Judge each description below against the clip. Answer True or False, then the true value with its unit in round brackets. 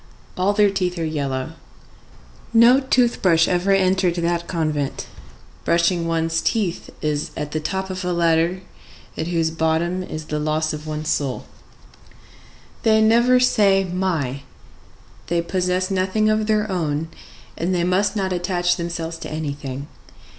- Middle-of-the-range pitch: True (175 Hz)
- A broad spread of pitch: False (3.1 semitones)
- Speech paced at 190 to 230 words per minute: False (145 wpm)